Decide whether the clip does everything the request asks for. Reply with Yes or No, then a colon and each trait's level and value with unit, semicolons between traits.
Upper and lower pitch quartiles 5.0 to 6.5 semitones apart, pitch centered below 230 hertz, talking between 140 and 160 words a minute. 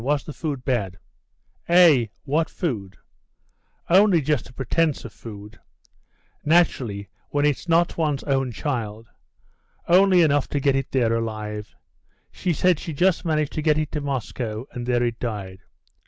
Yes: wide, 5.6 semitones; low, 135 Hz; average, 155 wpm